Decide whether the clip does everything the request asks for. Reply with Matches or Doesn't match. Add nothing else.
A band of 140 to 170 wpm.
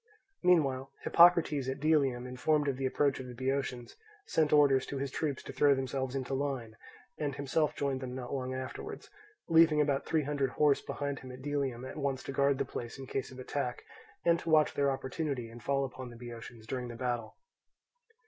Doesn't match